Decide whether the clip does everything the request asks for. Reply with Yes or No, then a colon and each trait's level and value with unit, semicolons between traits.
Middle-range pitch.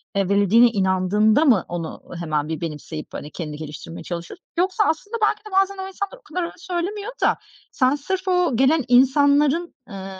No: very high, 260 Hz